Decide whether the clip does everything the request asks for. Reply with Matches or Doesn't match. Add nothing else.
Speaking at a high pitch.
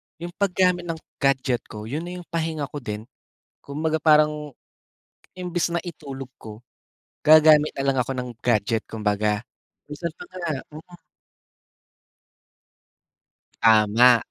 Doesn't match